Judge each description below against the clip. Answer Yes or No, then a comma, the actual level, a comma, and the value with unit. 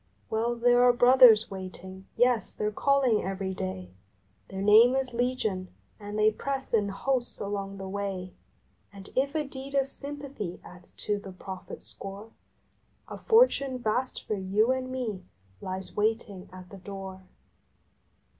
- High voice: Yes, high, 215 Hz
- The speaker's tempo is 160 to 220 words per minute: No, average, 150 wpm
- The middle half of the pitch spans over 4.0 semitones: Yes, average, 4.8 semitones